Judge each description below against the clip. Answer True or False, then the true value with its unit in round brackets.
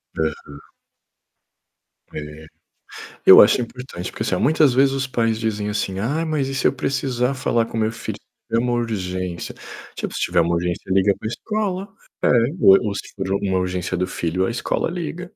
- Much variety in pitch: True (6.4 semitones)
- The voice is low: True (110 Hz)